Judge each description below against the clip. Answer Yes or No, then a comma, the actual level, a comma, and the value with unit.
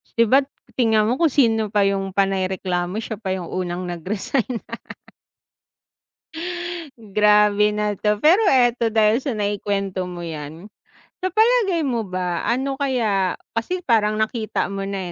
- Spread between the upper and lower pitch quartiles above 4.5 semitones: No, average, 3.8 semitones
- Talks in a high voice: Yes, high, 210 Hz